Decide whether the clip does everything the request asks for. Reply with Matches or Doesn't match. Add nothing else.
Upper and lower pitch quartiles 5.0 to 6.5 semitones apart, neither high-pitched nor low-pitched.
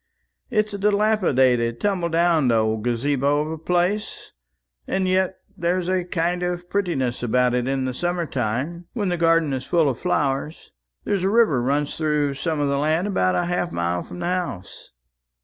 Matches